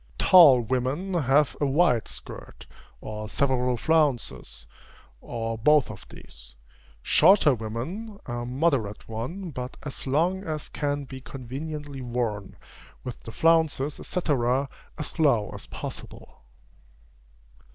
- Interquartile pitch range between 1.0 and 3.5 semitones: No, average, 4.6 semitones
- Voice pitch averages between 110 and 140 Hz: Yes, low, 135 Hz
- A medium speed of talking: No, slow, 115 wpm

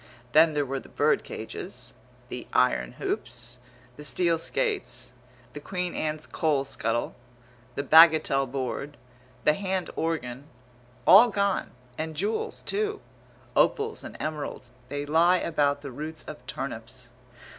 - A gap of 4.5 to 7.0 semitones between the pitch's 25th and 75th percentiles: No, average, 4.0 semitones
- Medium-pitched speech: Yes, medium, 155 Hz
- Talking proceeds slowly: Yes, slow, 130 wpm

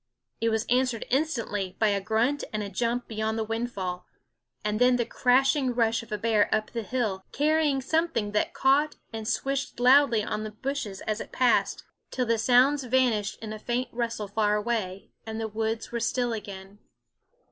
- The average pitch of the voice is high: Yes, high, 230 Hz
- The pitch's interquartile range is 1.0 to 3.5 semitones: Yes, average, 3.0 semitones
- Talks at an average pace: Yes, average, 180 wpm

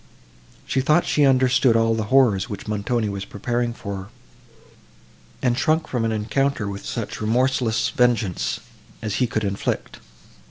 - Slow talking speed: No, average, 150 wpm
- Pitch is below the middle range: Yes, low, 115 Hz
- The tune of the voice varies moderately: Yes, average, 3.5 semitones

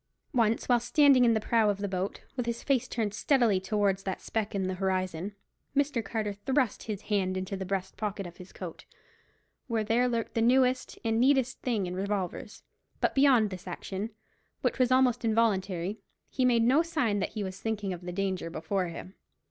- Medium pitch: No, high, 210 Hz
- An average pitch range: Yes, average, 4.1 semitones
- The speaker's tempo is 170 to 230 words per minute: Yes, average, 195 wpm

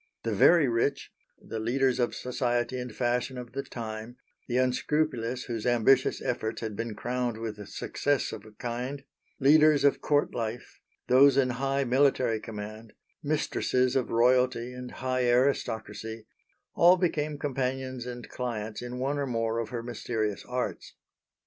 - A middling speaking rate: Yes, average, 150 wpm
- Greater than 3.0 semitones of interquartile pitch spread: No, narrow, 2.5 semitones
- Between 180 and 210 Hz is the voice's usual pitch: No, low, 125 Hz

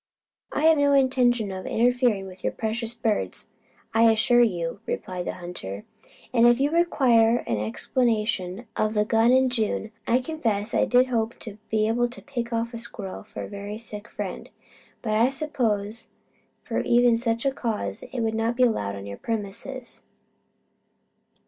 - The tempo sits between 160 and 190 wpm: Yes, average, 170 wpm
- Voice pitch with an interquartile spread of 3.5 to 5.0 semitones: No, average, 2.9 semitones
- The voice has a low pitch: No, high, 225 Hz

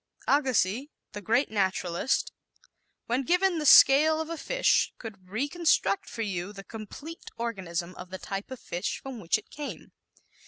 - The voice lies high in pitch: Yes, high, 230 Hz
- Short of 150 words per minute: No, average, 155 wpm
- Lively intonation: Yes, wide, 7.1 semitones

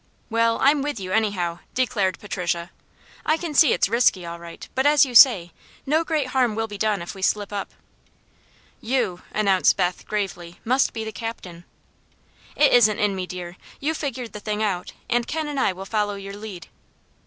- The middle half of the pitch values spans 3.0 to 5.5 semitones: Yes, average, 5.2 semitones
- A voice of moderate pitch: No, high, 210 Hz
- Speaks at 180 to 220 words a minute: Yes, average, 190 wpm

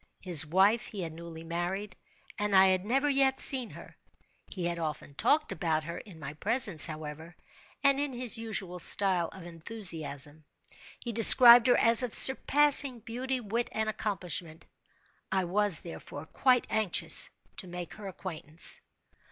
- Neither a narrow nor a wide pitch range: No, wide, 5.9 semitones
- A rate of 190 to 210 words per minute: No, average, 150 wpm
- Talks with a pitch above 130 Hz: Yes, high, 190 Hz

